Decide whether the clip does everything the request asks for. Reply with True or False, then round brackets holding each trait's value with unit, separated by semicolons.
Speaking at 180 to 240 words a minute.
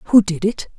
True (230 wpm)